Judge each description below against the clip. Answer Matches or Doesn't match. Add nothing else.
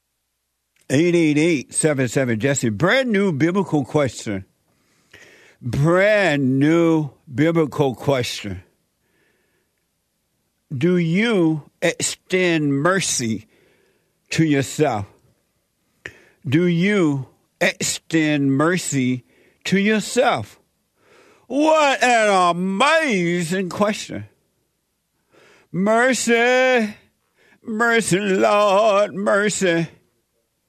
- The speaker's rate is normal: Doesn't match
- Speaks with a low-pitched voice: Doesn't match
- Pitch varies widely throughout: Matches